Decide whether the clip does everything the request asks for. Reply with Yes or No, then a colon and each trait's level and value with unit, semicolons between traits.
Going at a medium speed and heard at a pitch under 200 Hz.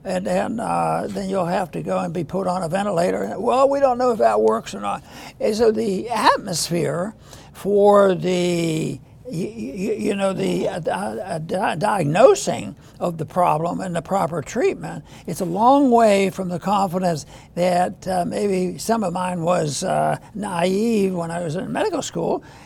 Yes: average, 165 wpm; medium, 185 Hz